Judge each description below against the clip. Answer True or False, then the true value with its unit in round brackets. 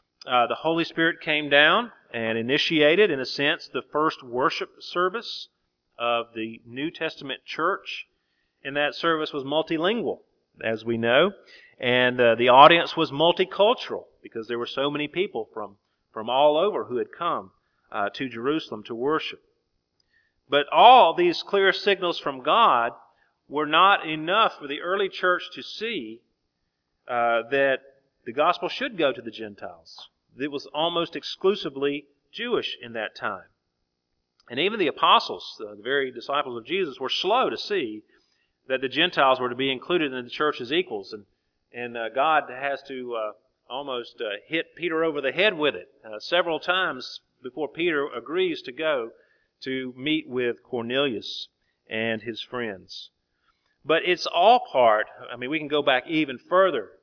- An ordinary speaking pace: True (160 wpm)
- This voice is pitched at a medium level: True (145 Hz)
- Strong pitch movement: True (6.8 semitones)